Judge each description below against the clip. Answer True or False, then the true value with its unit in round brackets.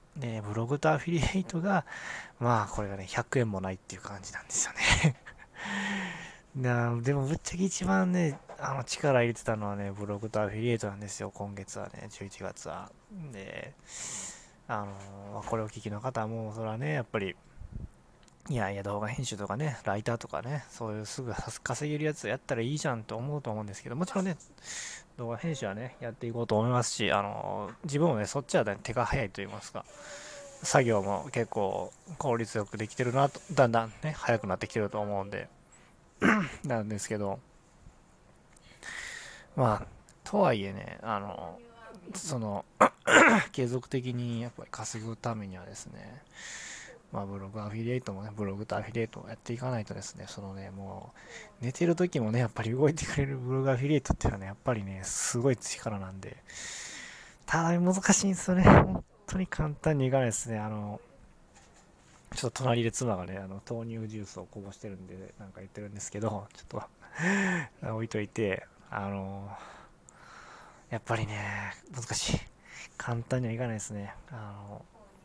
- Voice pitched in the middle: False (115 Hz)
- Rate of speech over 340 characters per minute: True (350 characters per minute)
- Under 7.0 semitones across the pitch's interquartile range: True (5.4 semitones)